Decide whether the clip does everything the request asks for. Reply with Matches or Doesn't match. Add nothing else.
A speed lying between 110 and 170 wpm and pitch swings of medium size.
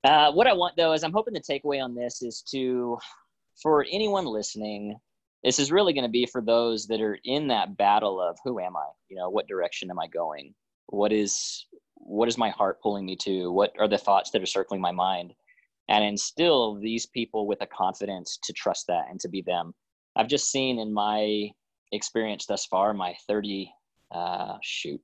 Doesn't match